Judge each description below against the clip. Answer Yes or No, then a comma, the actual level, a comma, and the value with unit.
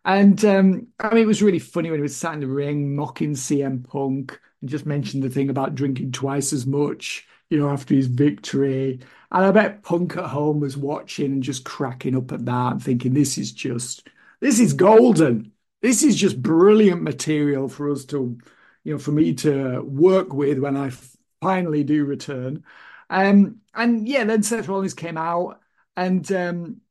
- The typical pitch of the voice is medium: Yes, medium, 150 Hz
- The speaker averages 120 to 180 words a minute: No, average, 190 wpm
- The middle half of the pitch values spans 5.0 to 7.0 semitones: Yes, wide, 5.5 semitones